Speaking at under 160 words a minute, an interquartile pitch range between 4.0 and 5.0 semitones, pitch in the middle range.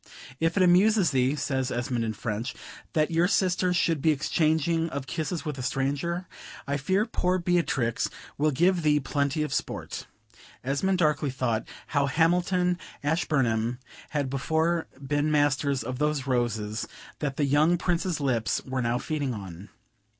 Yes: average, 150 wpm; average, 4.4 semitones; medium, 145 Hz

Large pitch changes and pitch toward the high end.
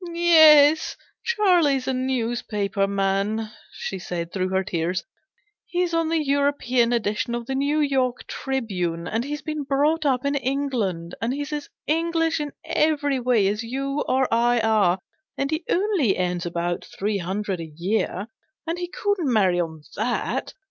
Yes: wide, 7.1 semitones; very high, 255 Hz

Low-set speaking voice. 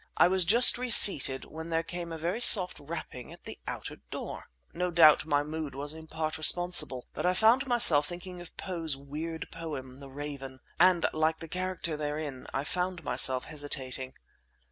No: medium, 160 Hz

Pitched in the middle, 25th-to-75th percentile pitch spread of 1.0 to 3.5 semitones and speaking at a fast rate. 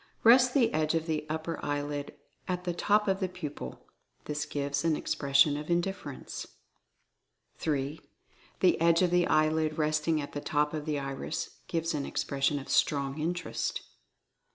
No: medium, 155 Hz; average, 2.9 semitones; average, 155 wpm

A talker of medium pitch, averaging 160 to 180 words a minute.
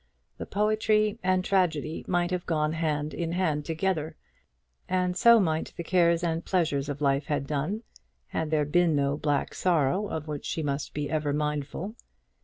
Yes: medium, 160 Hz; average, 170 wpm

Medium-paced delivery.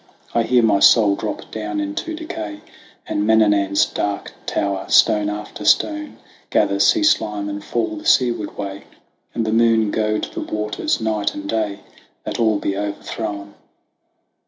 Yes: average, 150 wpm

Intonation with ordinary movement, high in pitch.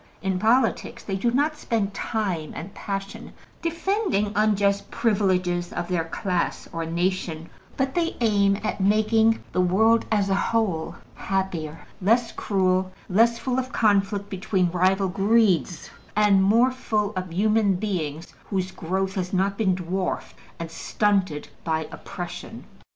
Yes: average, 3.1 semitones; high, 195 Hz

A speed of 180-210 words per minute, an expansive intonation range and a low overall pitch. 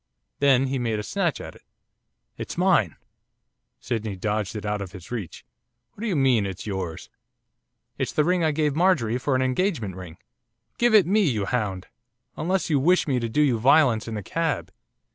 Yes: average, 190 wpm; wide, 7.0 semitones; low, 125 Hz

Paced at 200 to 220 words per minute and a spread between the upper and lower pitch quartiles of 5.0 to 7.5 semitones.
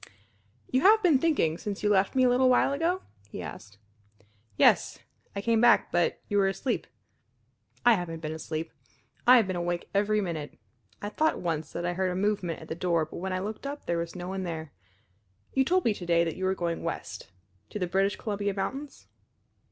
Yes: fast, 205 wpm; wide, 5.6 semitones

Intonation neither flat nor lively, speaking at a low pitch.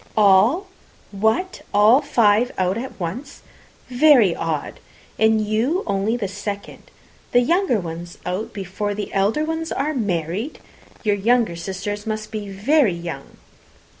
No: average, 4.1 semitones; high, 210 Hz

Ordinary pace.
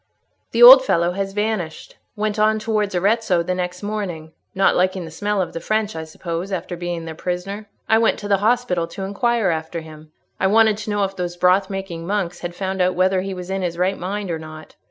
No: fast, 220 wpm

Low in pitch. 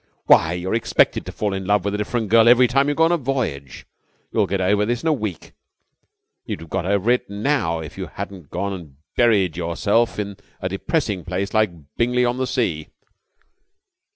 Yes: low, 100 Hz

